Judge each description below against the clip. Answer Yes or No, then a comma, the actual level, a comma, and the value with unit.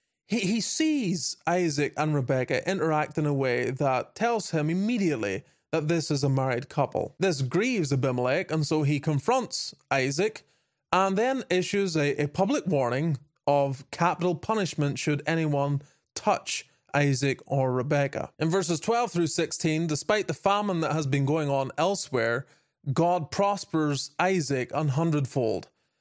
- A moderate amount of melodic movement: Yes, average, 4.3 semitones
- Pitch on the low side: No, medium, 155 Hz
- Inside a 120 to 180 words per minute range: Yes, average, 140 wpm